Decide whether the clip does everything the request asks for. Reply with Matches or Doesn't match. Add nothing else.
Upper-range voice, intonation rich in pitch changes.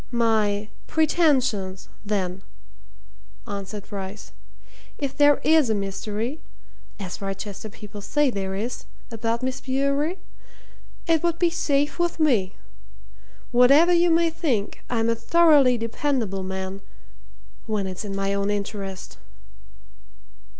Matches